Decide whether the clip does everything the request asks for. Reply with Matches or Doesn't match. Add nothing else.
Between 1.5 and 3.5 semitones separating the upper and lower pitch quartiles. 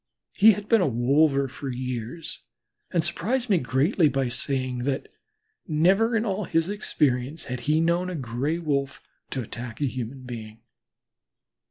Doesn't match